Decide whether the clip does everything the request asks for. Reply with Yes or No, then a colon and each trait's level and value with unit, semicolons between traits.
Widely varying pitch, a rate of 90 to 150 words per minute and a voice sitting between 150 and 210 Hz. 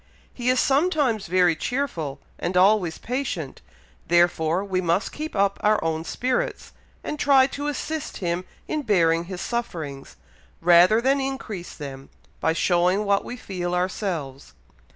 Yes: wide, 6.8 semitones; average, 140 wpm; medium, 185 Hz